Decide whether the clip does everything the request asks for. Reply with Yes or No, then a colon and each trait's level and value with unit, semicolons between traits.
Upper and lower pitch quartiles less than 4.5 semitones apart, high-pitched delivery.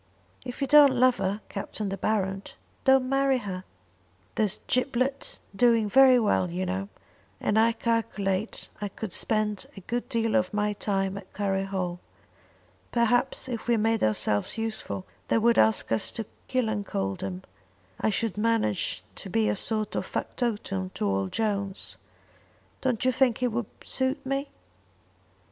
Yes: average, 3.9 semitones; high, 215 Hz